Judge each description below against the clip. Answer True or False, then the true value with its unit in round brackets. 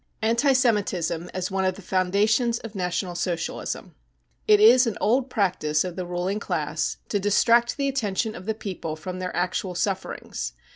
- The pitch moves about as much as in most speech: True (4.2 semitones)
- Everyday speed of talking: True (165 wpm)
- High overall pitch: True (195 Hz)